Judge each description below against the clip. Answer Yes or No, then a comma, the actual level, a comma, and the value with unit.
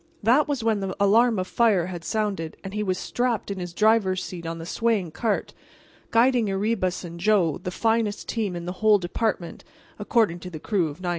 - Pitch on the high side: Yes, high, 200 Hz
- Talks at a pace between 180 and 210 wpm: Yes, average, 200 wpm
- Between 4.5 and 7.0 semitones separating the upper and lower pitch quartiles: No, average, 3.9 semitones